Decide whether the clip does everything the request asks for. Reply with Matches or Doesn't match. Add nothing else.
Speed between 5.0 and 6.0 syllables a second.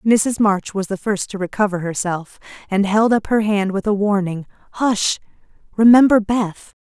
Doesn't match